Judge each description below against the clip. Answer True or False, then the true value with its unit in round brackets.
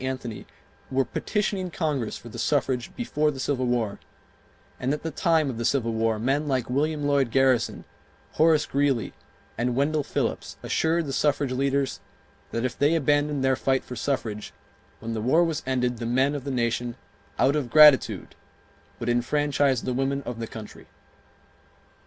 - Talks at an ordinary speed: True (165 wpm)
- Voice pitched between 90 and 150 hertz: True (135 Hz)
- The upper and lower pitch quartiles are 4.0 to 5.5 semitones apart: False (3.3 semitones)